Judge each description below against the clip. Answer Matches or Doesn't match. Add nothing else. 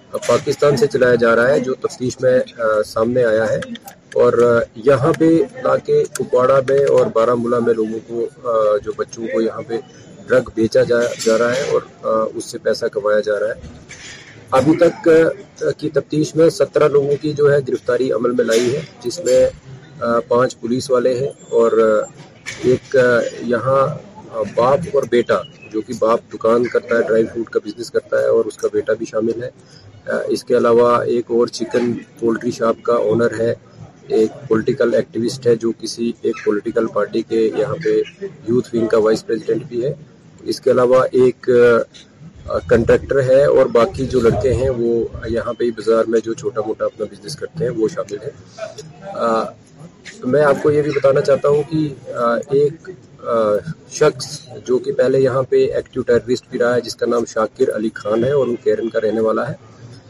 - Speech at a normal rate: Matches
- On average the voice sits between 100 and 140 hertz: Matches